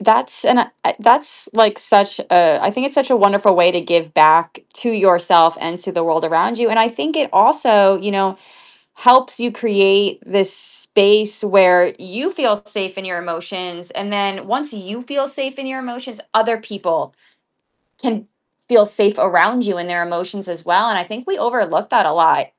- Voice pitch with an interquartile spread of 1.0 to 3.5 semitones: No, average, 4.6 semitones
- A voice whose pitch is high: Yes, high, 200 Hz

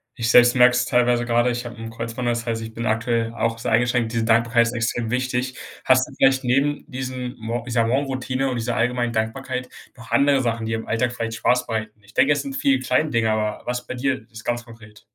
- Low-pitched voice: Yes, low, 120 Hz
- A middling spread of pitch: No, narrow, 1.9 semitones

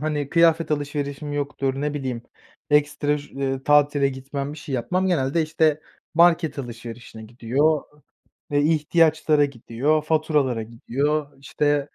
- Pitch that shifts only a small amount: Yes, narrow, 2.2 semitones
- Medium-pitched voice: Yes, medium, 145 Hz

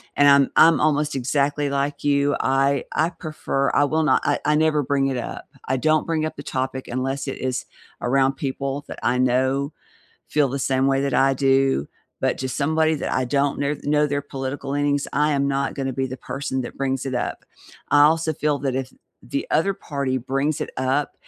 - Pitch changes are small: Yes, narrow, 1.7 semitones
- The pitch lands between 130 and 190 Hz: Yes, medium, 140 Hz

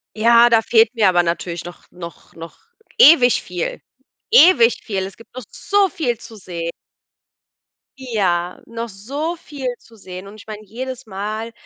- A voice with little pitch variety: No, average, 4.9 semitones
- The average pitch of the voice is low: No, high, 220 Hz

